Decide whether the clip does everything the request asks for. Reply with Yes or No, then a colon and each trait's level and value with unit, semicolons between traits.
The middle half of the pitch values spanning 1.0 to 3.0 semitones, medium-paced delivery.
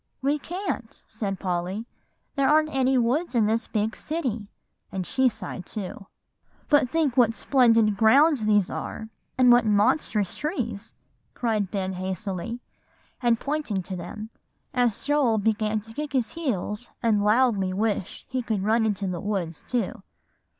No: average, 4.1 semitones; average, 150 wpm